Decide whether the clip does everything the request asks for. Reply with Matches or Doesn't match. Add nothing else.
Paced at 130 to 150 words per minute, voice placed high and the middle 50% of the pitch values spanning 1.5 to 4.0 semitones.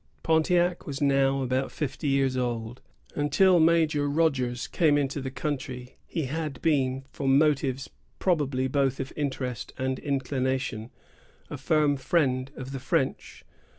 Doesn't match